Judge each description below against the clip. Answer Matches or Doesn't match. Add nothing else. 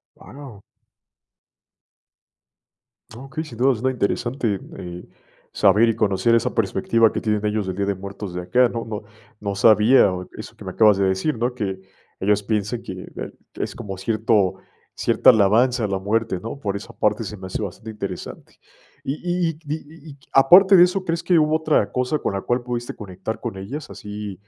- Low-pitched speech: Matches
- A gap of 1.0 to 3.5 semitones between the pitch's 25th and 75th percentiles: Doesn't match